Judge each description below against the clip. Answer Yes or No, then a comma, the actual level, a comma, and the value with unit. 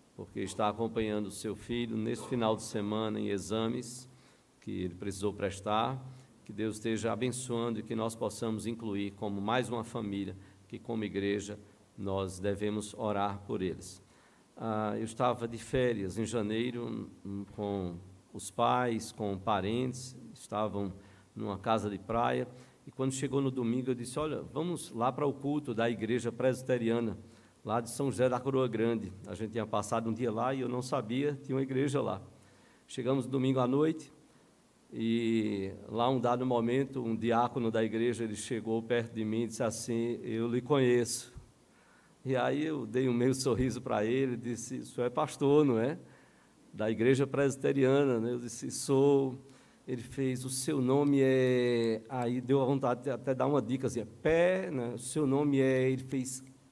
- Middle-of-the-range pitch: No, low, 120 Hz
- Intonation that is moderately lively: Yes, average, 3.0 semitones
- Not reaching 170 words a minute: No, average, 175 wpm